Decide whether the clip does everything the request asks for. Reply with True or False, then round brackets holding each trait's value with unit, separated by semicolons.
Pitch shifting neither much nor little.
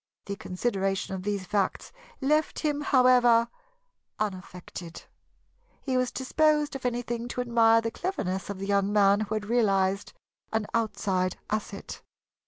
True (4.0 semitones)